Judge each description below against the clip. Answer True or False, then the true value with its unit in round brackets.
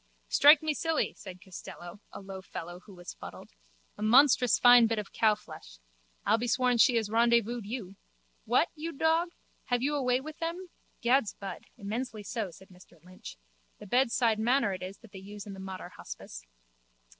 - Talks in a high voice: True (225 Hz)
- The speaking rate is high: False (180 wpm)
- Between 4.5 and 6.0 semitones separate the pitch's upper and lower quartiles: True (4.8 semitones)